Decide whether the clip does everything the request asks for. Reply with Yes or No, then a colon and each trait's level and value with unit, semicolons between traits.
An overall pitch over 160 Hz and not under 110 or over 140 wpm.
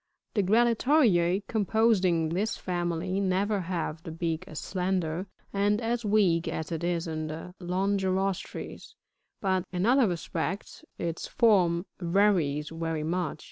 Yes: medium, 185 Hz; slow, 135 wpm